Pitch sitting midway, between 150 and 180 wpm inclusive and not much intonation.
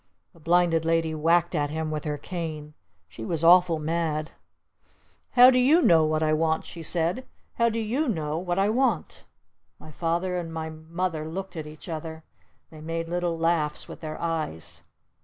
Yes: medium, 165 Hz; average, 175 wpm; narrow, 2.2 semitones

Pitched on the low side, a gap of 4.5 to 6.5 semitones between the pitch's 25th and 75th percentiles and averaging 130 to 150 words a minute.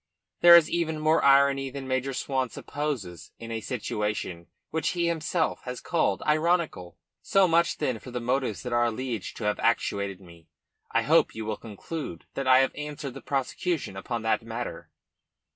No: low, 130 Hz; wide, 5.5 semitones; average, 170 wpm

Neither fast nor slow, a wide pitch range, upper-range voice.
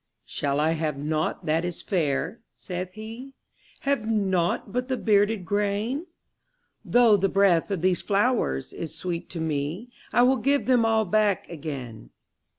Yes: average, 155 wpm; wide, 5.7 semitones; high, 195 Hz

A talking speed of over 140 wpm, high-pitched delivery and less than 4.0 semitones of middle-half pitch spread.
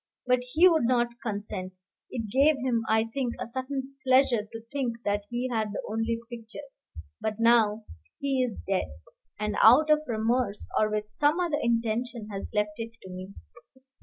Yes: average, 170 wpm; high, 235 Hz; average, 3.3 semitones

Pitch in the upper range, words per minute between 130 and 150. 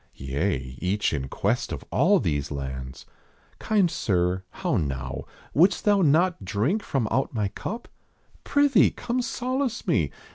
No: low, 105 Hz; average, 140 wpm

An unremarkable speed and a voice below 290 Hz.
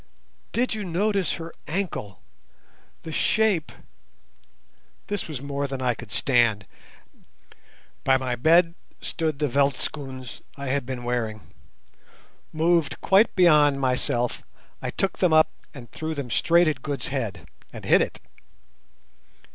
No: slow, 125 wpm; medium, 140 Hz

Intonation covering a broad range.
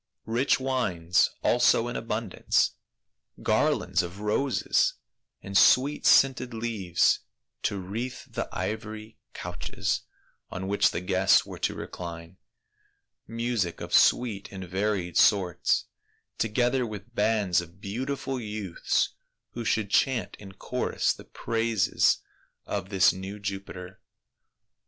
No: average, 3.8 semitones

